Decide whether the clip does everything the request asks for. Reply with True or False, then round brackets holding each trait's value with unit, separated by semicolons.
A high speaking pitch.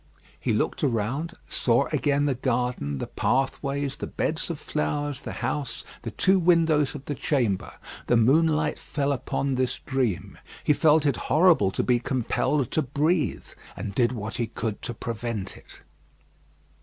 False (135 Hz)